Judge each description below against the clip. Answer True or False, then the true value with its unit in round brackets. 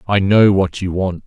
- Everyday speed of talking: False (235 wpm)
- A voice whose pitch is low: True (95 Hz)